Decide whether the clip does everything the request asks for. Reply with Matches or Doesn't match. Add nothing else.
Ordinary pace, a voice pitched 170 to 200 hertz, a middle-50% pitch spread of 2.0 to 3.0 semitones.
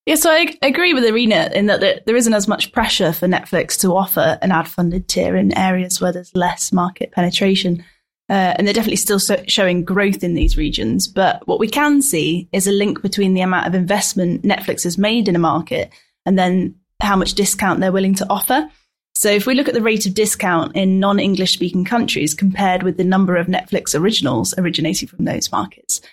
Doesn't match